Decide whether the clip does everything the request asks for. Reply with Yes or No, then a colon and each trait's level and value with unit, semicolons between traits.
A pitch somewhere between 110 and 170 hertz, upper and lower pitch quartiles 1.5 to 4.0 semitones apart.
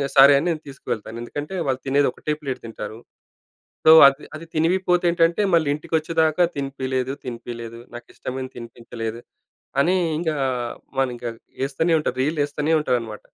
No: medium, 140 Hz; average, 4.5 semitones